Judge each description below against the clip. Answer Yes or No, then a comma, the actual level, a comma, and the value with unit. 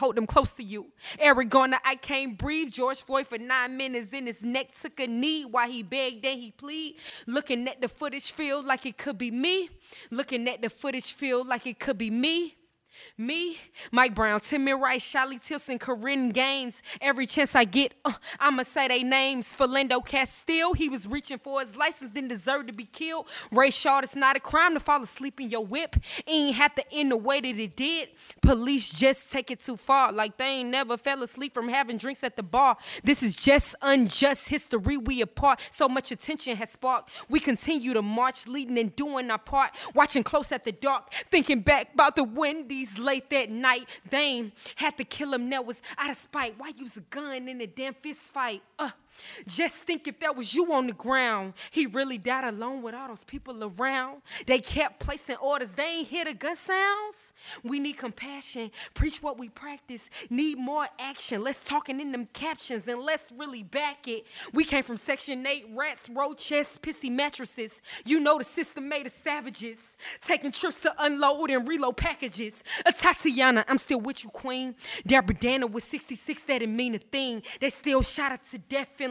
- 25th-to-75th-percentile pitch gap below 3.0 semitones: Yes, narrow, 2.5 semitones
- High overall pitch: Yes, very high, 270 Hz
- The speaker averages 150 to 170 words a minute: No, fast, 205 wpm